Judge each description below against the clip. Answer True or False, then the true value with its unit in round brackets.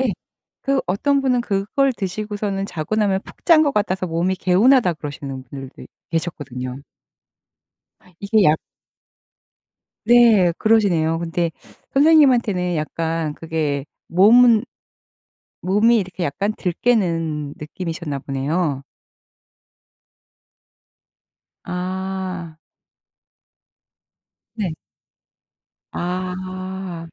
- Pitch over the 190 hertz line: False (185 Hz)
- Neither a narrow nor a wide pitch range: True (4.6 semitones)